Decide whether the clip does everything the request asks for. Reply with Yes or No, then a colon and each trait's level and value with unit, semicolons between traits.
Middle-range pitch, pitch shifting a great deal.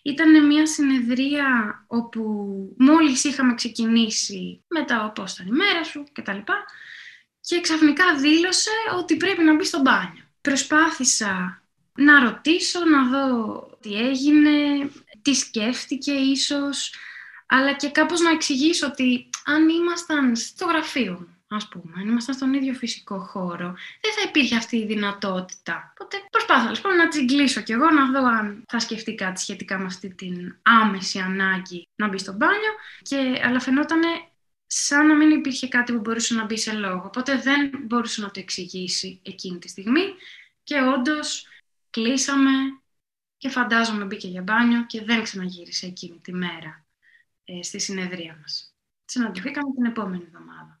No: very high, 255 Hz; wide, 6.6 semitones